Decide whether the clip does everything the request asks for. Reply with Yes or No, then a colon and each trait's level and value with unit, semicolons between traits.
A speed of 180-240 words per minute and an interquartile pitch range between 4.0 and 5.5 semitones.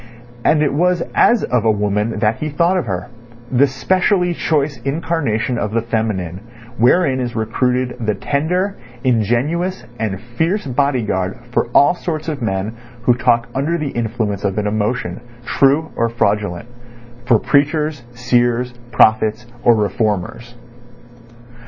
No: slow, 135 wpm; average, 5.0 semitones